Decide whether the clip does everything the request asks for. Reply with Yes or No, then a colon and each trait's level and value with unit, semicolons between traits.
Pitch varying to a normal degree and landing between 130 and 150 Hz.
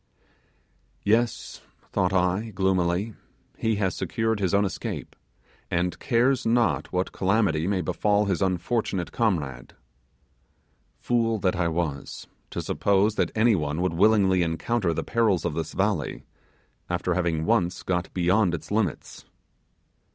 No: average, 4.0 semitones; very low, 95 Hz